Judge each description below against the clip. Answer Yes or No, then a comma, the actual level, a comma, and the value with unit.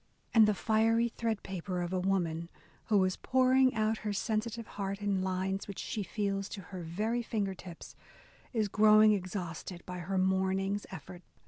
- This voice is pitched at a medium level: No, high, 195 Hz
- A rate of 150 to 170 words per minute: Yes, average, 165 wpm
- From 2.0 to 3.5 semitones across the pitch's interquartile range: Yes, narrow, 2.6 semitones